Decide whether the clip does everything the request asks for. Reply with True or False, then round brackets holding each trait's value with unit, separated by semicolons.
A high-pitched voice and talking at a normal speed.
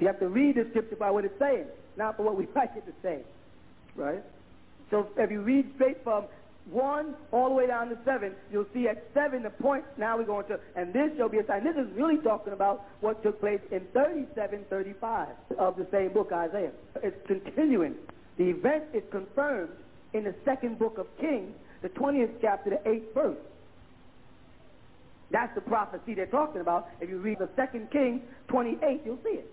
True (225 Hz; 195 wpm)